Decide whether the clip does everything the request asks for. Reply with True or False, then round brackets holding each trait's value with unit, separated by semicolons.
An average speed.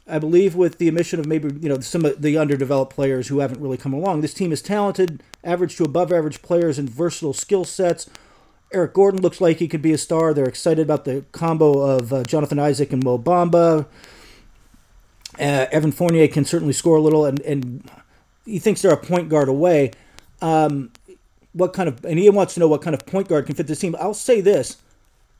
False (215 wpm)